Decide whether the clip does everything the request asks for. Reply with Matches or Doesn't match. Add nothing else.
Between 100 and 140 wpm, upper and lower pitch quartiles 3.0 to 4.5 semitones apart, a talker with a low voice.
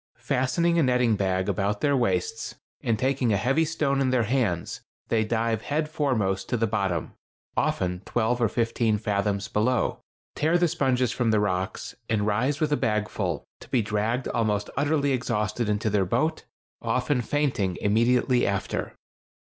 Doesn't match